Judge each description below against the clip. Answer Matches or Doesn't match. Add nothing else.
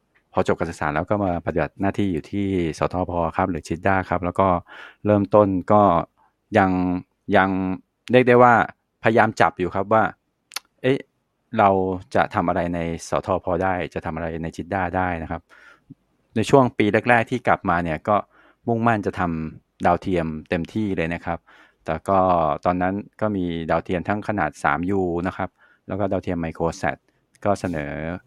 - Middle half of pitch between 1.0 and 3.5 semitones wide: Matches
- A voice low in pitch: Matches